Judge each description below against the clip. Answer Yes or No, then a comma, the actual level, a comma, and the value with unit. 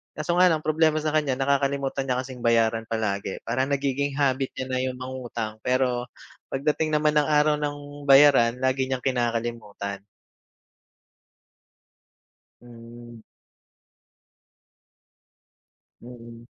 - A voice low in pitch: Yes, low, 130 Hz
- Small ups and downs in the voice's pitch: No, average, 3.3 semitones